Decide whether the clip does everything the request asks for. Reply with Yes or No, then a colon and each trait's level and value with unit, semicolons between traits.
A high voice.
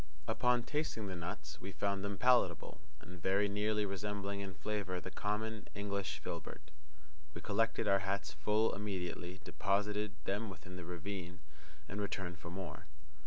No: low, 100 Hz